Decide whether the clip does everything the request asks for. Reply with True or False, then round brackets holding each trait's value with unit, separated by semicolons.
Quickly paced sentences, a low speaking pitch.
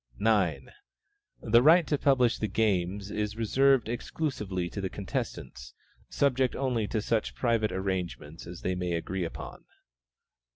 False (135 wpm; 105 Hz)